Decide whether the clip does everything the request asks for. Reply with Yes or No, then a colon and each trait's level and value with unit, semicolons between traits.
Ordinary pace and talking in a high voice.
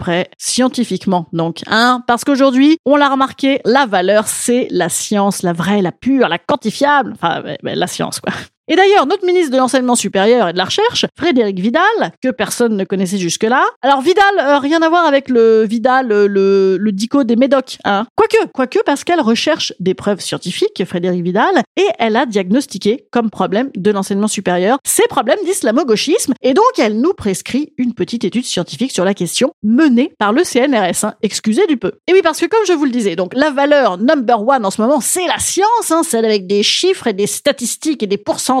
Yes: average, 210 wpm; high, 245 Hz